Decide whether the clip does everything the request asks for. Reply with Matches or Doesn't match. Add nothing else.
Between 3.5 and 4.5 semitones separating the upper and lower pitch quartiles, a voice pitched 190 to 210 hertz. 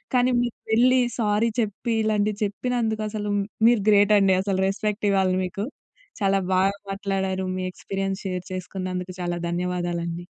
Doesn't match